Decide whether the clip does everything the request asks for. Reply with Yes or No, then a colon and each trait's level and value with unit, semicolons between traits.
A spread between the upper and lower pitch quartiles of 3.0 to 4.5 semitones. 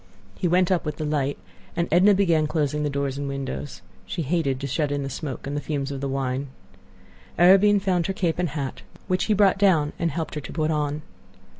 Yes: average, 4.0 semitones